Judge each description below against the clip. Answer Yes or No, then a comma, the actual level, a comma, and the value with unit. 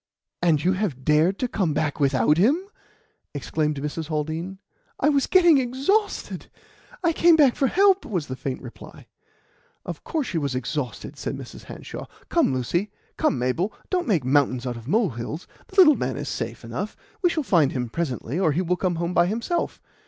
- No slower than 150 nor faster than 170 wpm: No, average, 180 wpm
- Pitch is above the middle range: No, medium, 170 Hz